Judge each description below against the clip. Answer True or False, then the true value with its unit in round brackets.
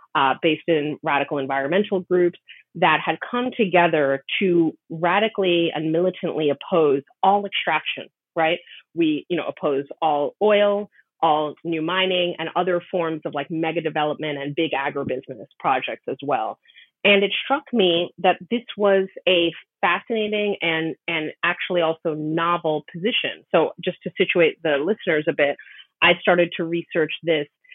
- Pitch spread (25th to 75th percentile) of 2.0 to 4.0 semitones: True (3.4 semitones)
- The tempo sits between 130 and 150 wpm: True (145 wpm)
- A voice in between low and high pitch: True (170 Hz)